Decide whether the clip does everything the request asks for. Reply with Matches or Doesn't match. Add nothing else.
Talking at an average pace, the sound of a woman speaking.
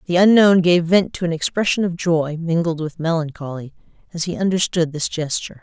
Matches